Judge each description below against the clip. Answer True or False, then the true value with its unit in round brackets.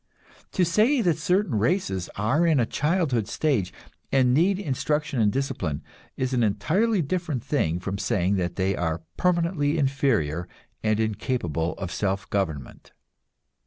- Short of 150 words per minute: True (135 wpm)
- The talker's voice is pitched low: True (125 Hz)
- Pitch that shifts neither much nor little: False (8.7 semitones)